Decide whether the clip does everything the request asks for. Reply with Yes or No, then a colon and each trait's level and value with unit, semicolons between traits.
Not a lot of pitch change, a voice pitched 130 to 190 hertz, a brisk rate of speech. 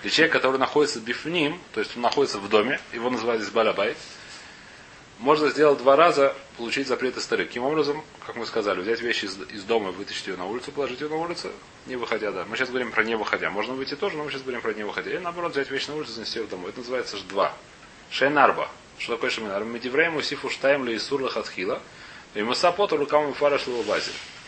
No: average, 3.5 semitones; medium, 140 Hz; fast, 220 wpm